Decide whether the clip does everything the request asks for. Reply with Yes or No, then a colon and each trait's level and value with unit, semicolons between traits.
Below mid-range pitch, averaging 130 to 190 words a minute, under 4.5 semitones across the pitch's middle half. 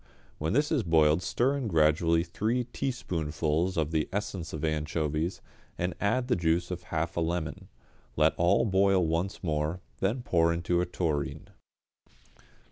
Yes: very low, 85 Hz; average, 150 wpm; average, 3.5 semitones